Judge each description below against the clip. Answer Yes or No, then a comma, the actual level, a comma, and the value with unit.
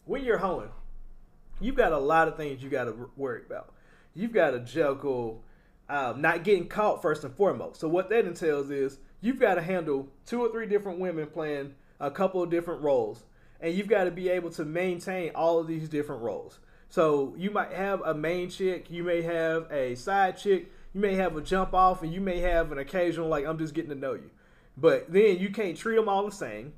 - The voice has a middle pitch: Yes, medium, 170 Hz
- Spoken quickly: Yes, fast, 220 wpm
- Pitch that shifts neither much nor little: Yes, average, 3.8 semitones